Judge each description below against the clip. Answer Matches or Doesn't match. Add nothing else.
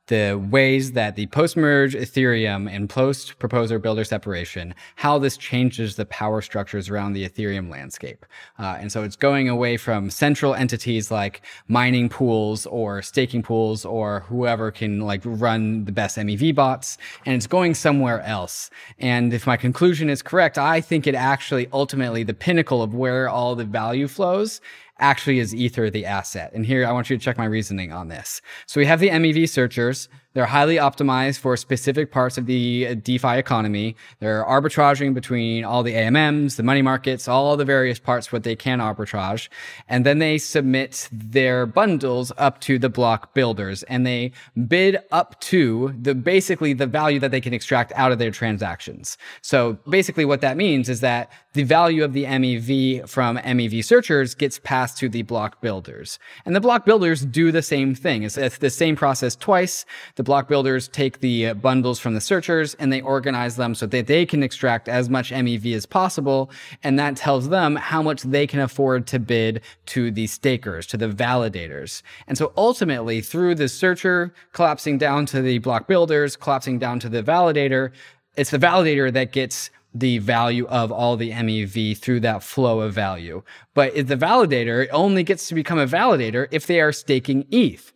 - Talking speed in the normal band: Matches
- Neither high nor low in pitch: Doesn't match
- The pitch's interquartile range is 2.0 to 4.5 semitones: Matches